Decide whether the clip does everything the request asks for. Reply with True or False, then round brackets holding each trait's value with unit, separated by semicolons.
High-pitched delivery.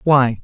False (130 Hz)